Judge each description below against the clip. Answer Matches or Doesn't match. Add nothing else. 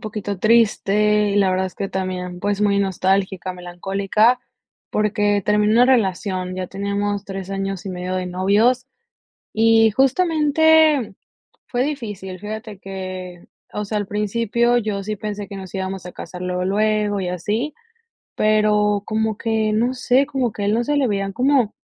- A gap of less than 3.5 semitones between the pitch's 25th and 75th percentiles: Matches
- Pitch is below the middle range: Doesn't match